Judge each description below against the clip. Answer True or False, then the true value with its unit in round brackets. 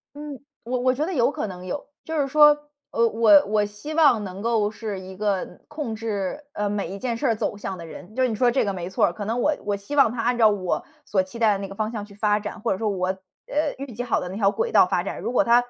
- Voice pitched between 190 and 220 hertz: True (215 Hz)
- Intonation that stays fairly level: False (3.9 semitones)